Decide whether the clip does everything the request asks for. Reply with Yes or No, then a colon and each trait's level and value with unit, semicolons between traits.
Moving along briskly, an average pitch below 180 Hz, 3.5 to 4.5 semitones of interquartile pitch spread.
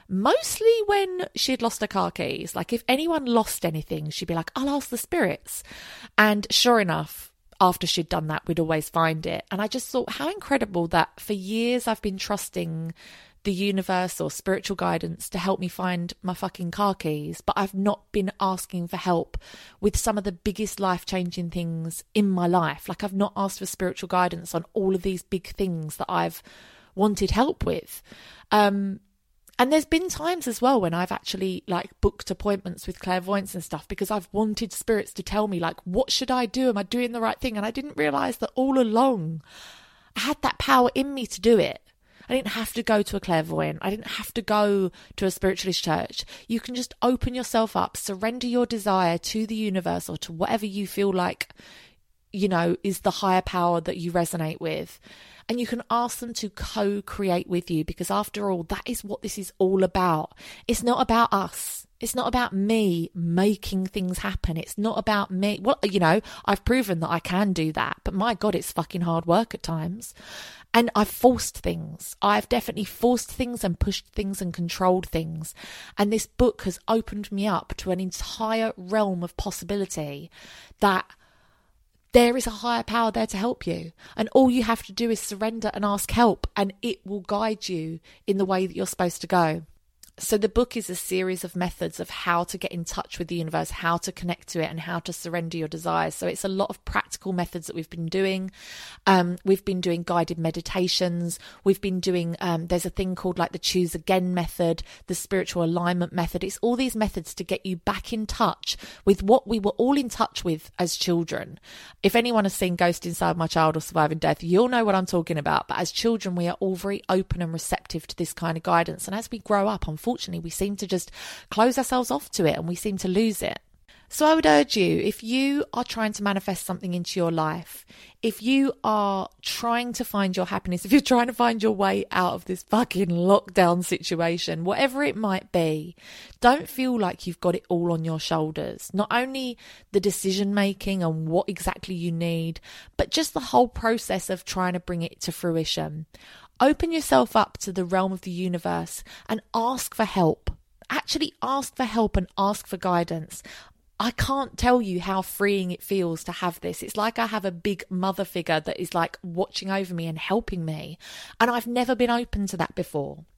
No: fast, 210 wpm; high, 195 Hz; average, 4.1 semitones